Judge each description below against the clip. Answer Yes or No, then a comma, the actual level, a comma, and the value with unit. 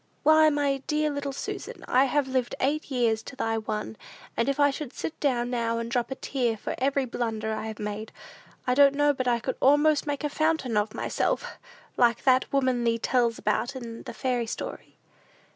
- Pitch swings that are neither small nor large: Yes, average, 3.5 semitones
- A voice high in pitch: Yes, very high, 255 Hz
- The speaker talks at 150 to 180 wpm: No, average, 200 wpm